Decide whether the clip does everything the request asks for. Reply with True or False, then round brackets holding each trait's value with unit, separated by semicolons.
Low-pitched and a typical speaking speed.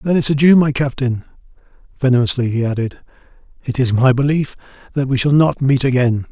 True (130 Hz; 170 wpm)